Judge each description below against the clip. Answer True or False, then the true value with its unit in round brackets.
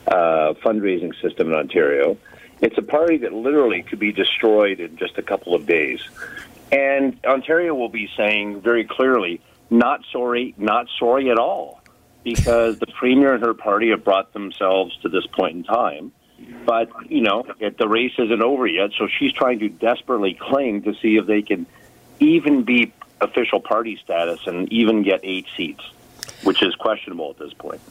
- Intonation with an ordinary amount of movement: True (4.1 semitones)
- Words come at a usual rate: True (175 wpm)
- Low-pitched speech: True (115 Hz)